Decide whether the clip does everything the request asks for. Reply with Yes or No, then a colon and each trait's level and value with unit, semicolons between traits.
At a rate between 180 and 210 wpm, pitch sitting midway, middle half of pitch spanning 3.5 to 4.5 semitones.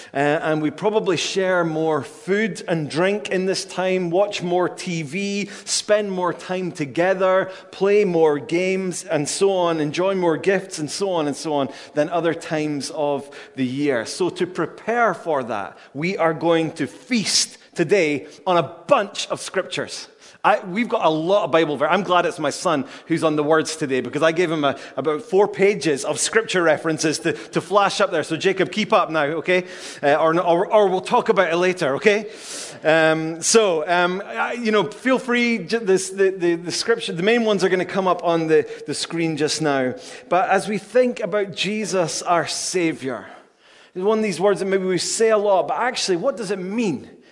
Yes: average, 200 wpm; medium, 180 Hz; average, 3.9 semitones